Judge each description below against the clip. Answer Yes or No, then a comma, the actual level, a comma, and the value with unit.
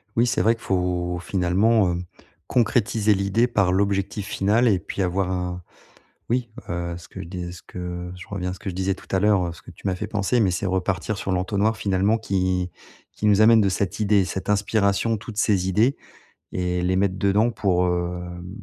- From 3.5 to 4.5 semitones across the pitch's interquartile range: No, average, 2.7 semitones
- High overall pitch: No, very low, 95 Hz